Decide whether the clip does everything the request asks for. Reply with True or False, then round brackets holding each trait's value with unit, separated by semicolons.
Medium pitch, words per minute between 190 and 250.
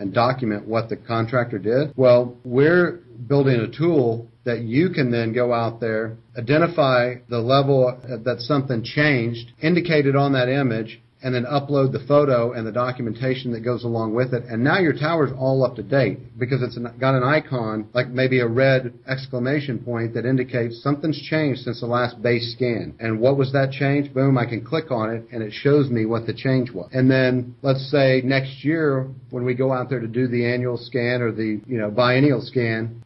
False (125 Hz; 200 wpm)